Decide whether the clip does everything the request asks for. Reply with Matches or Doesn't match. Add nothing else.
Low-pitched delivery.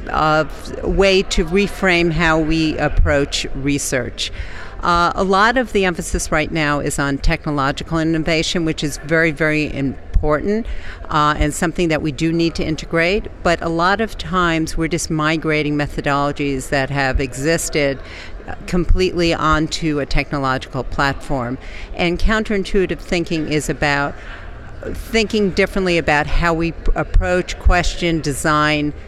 Doesn't match